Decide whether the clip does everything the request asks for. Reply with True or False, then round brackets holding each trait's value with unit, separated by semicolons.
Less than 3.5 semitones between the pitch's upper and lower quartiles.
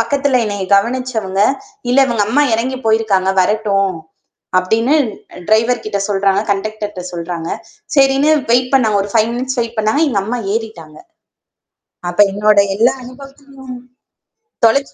False (4.0 semitones)